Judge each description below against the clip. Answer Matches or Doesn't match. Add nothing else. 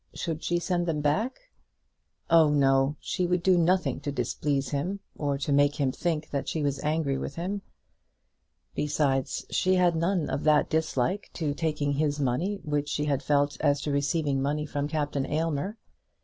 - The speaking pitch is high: Doesn't match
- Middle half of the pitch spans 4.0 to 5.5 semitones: Doesn't match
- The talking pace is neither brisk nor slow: Matches